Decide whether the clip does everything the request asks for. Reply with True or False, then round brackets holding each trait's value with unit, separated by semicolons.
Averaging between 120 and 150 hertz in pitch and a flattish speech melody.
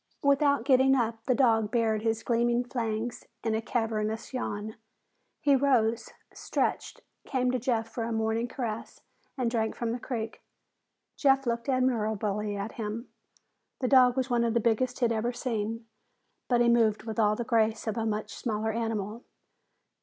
False (230 Hz; 2.1 semitones)